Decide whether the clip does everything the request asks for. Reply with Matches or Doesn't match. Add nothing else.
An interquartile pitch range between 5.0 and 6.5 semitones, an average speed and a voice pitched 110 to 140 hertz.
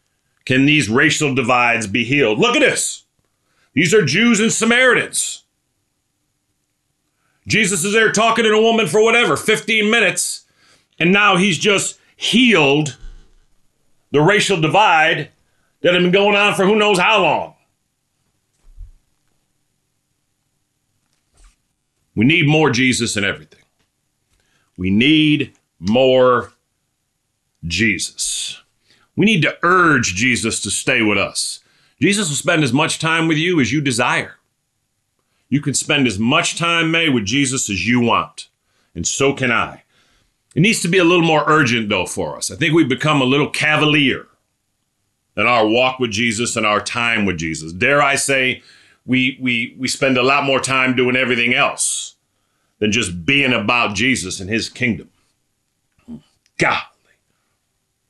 Matches